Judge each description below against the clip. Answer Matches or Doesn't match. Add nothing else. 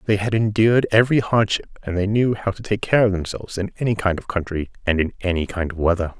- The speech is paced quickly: Matches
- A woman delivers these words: Doesn't match